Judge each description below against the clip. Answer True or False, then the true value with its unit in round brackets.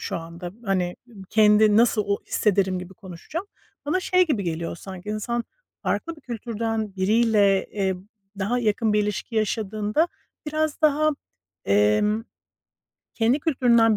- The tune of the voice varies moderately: True (3.7 semitones)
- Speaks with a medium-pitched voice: False (215 Hz)